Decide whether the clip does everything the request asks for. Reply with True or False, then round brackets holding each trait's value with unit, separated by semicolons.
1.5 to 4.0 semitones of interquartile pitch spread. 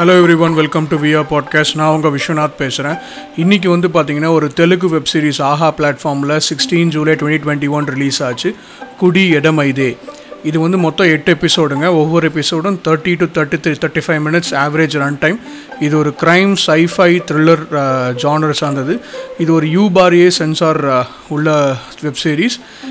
True (2.5 semitones)